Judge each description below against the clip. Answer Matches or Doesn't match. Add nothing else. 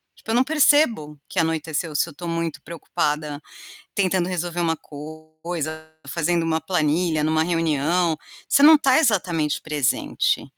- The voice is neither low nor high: Matches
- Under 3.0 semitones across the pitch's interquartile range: Matches